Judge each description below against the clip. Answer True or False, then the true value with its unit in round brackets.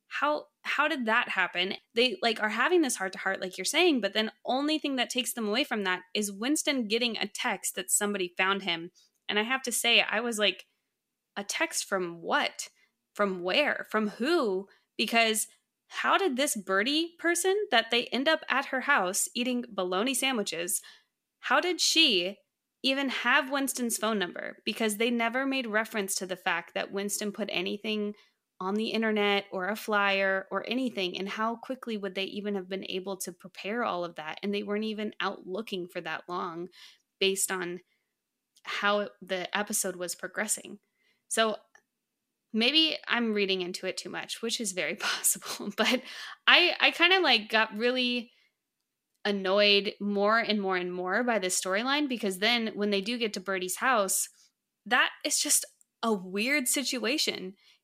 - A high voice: True (215 Hz)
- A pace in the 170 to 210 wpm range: True (175 wpm)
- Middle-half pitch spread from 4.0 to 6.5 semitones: True (4.4 semitones)